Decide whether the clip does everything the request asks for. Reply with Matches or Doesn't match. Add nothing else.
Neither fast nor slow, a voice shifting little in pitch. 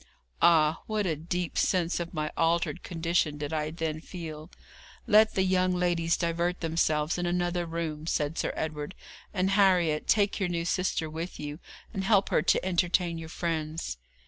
Matches